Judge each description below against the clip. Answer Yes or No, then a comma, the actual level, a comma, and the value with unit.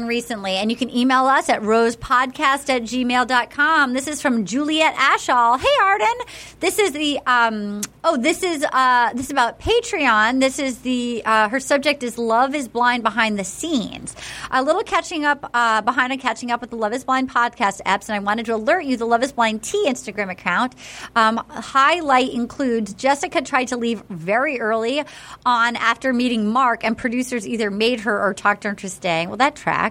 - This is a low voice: No, high, 245 Hz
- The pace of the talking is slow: No, average, 195 wpm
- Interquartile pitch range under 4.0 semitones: Yes, average, 3.3 semitones